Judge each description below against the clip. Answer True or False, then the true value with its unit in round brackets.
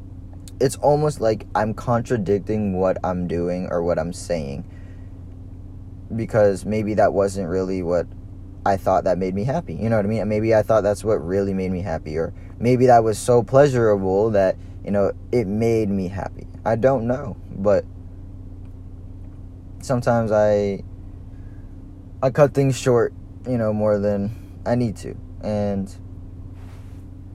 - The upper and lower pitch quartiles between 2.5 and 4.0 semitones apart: True (3.0 semitones)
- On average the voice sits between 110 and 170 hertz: False (95 Hz)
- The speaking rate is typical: True (150 wpm)